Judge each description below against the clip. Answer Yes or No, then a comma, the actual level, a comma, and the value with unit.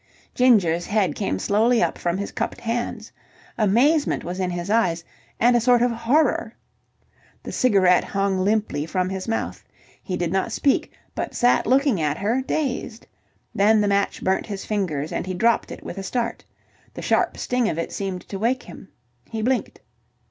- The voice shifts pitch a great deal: No, average, 4.5 semitones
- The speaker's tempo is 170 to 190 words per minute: Yes, average, 175 wpm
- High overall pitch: Yes, high, 205 Hz